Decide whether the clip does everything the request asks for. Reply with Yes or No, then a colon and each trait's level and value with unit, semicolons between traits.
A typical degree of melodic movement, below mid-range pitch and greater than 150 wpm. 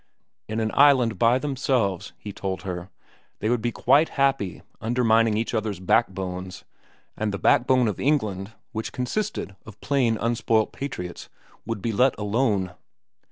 No: average, 4.1 semitones; low, 115 Hz; average, 145 wpm